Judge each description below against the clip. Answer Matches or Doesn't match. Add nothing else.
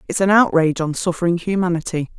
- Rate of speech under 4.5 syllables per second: Doesn't match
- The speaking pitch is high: Doesn't match